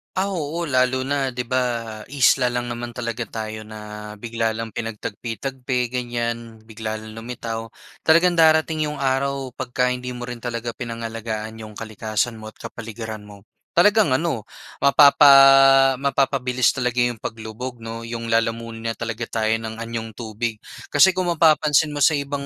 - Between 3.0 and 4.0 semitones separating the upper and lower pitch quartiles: Yes, average, 3.3 semitones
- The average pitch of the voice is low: Yes, low, 120 Hz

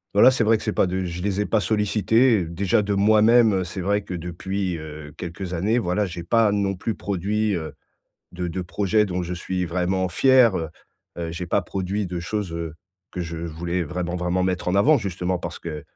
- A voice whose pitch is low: Yes, very low, 95 Hz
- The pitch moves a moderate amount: Yes, average, 3.1 semitones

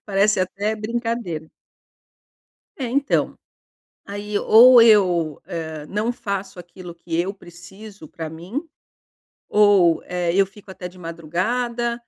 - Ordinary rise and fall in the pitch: Yes, average, 4.2 semitones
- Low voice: No, high, 195 Hz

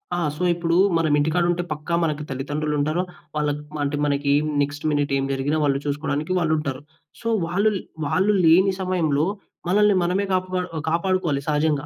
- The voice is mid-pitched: Yes, medium, 155 Hz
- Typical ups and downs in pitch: Yes, average, 3.4 semitones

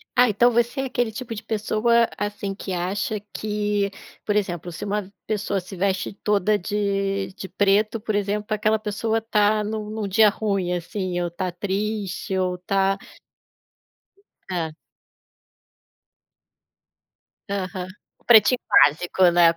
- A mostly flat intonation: Yes, narrow, 2.2 semitones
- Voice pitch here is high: Yes, high, 205 Hz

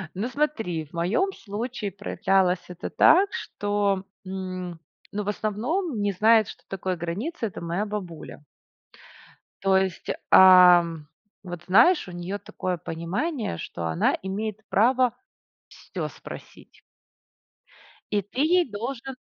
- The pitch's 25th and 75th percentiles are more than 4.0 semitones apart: Yes, average, 4.4 semitones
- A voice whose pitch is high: Yes, high, 200 Hz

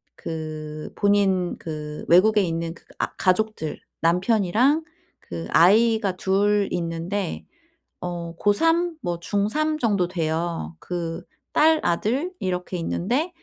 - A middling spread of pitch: Yes, average, 4.5 semitones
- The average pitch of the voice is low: No, medium, 185 Hz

